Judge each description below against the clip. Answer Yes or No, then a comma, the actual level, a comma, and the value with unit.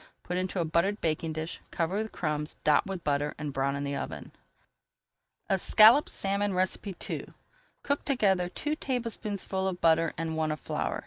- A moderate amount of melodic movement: Yes, average, 4.3 semitones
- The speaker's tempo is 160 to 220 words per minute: Yes, average, 165 wpm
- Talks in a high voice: No, medium, 180 Hz